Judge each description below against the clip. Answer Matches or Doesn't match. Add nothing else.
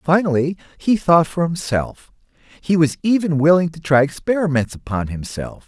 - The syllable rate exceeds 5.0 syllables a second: Doesn't match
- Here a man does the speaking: Matches